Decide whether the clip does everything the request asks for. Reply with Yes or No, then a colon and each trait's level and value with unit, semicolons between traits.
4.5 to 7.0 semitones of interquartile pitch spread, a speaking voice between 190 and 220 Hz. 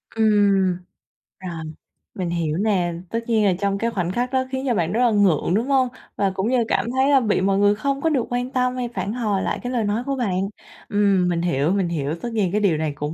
Yes: average, 5.0 semitones; high, 205 Hz